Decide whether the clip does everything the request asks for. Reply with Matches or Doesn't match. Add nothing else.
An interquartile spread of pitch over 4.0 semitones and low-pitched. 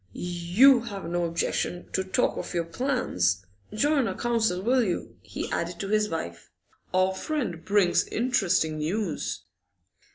Doesn't match